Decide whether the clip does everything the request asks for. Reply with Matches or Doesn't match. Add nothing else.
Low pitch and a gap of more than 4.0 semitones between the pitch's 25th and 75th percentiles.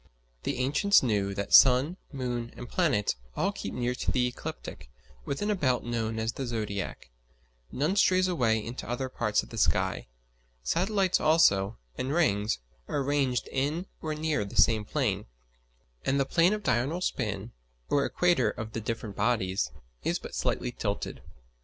Matches